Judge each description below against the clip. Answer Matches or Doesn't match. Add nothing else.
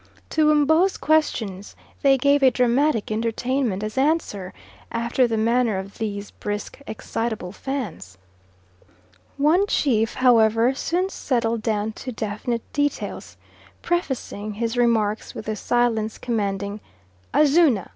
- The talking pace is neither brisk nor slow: Doesn't match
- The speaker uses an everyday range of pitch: Matches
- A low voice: Doesn't match